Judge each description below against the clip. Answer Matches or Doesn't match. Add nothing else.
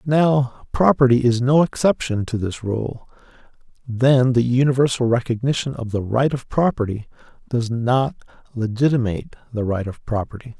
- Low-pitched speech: Matches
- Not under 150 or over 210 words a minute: Doesn't match